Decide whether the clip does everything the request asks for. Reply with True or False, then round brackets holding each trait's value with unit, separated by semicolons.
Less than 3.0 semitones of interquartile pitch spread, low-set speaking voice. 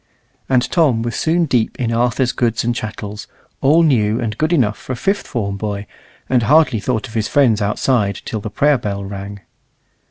False (4.1 semitones; 115 Hz)